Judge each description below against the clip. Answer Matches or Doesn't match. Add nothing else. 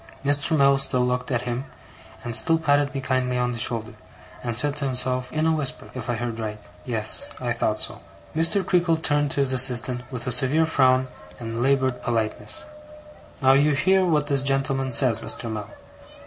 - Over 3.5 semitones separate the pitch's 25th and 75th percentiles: Doesn't match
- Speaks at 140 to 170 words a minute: Doesn't match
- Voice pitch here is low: Matches